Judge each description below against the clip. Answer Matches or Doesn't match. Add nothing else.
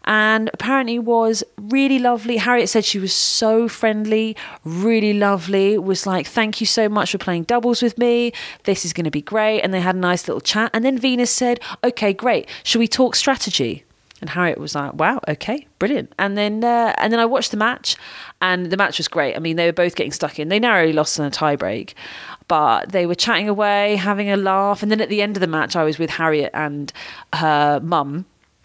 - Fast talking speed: Matches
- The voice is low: Doesn't match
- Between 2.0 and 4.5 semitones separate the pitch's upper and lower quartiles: Doesn't match